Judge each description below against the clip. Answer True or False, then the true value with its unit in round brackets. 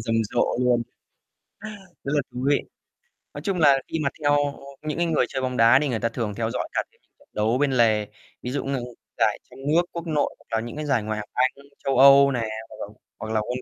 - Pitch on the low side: True (130 Hz)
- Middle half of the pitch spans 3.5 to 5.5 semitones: True (4.0 semitones)